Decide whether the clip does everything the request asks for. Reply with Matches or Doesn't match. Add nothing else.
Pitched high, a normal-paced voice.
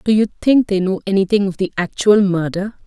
Doesn't match